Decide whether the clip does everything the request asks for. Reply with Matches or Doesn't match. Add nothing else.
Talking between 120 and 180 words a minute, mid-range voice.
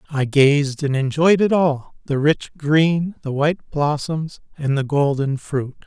Matches